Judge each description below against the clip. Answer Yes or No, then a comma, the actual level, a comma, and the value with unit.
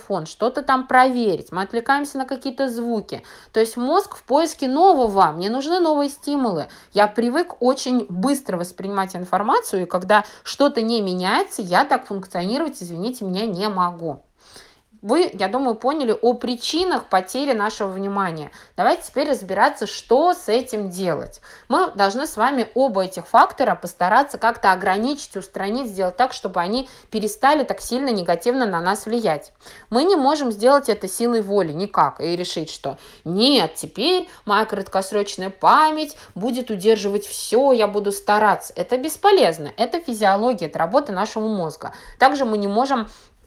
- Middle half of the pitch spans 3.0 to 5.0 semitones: No, wide, 5.6 semitones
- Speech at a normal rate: Yes, average, 150 wpm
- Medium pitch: No, high, 225 Hz